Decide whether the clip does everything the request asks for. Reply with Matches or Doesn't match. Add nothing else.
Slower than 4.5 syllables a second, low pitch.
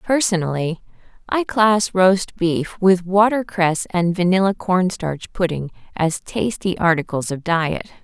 Doesn't match